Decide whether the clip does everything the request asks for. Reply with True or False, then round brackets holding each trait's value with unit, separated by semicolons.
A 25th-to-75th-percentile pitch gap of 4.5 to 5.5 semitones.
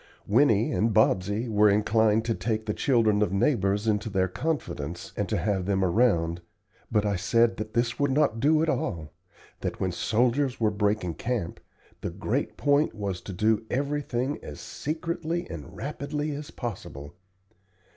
True (5.0 semitones)